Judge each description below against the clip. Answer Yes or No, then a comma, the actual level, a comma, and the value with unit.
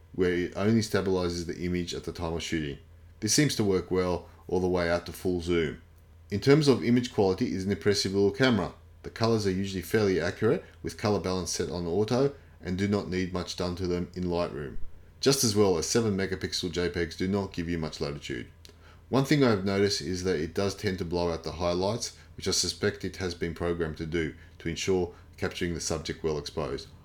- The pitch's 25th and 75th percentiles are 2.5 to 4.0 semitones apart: Yes, average, 2.8 semitones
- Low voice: Yes, very low, 90 Hz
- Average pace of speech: No, fast, 220 wpm